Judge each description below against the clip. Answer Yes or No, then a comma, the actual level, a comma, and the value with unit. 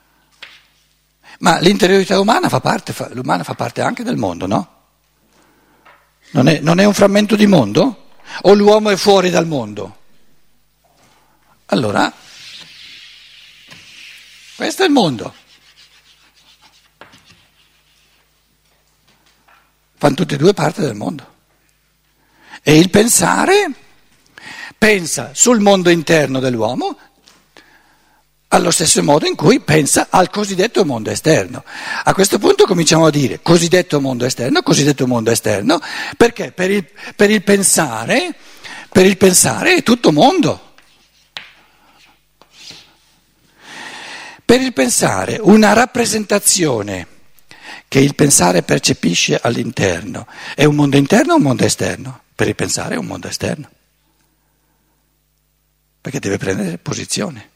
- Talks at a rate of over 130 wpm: No, slow, 115 wpm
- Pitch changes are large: Yes, wide, 6.7 semitones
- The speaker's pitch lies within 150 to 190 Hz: Yes, medium, 185 Hz